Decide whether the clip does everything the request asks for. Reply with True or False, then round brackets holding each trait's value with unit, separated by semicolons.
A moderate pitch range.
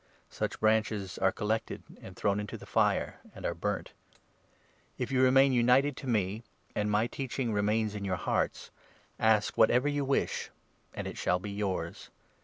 True (3.5 semitones)